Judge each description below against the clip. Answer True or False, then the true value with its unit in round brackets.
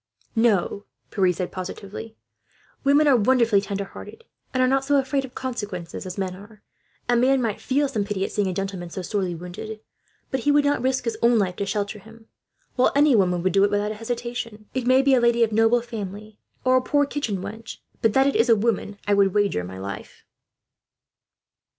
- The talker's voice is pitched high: True (220 Hz)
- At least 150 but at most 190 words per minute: False (205 wpm)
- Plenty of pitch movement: False (4.4 semitones)